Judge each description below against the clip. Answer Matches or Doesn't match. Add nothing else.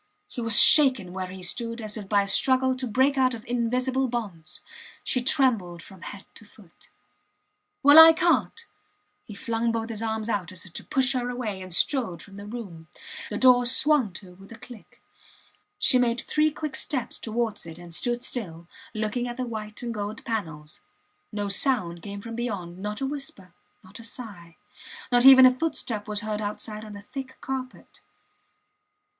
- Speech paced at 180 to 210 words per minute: Matches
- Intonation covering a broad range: Doesn't match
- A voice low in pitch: Doesn't match